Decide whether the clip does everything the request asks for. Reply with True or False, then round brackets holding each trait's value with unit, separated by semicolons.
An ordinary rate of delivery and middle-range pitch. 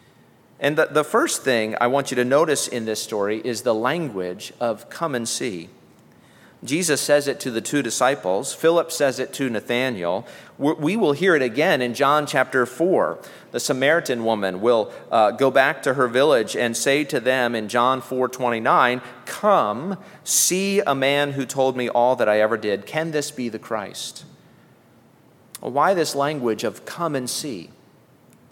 False (170 wpm; 130 Hz)